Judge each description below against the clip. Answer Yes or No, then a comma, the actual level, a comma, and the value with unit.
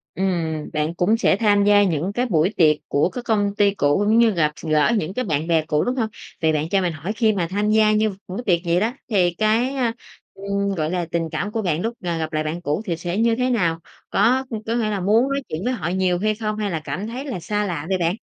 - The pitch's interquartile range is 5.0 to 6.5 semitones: No, average, 4.6 semitones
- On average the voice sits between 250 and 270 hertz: No, high, 195 Hz